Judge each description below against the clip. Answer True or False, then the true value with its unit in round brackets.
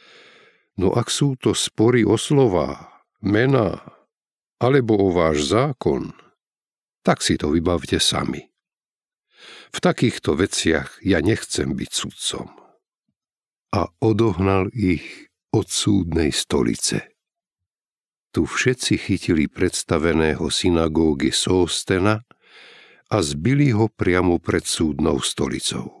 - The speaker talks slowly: True (100 wpm)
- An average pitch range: False (8.3 semitones)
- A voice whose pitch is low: True (110 Hz)